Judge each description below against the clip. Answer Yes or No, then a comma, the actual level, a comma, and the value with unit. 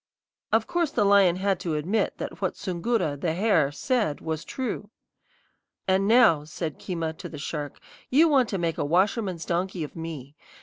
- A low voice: No, medium, 180 Hz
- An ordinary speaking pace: Yes, average, 175 wpm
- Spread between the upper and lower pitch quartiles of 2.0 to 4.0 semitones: No, average, 5.1 semitones